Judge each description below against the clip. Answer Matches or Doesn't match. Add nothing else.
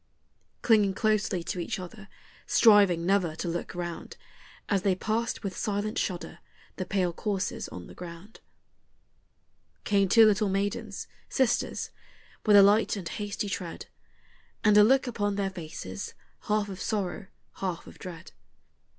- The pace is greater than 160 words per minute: Doesn't match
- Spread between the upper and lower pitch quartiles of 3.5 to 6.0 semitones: Doesn't match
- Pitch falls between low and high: Doesn't match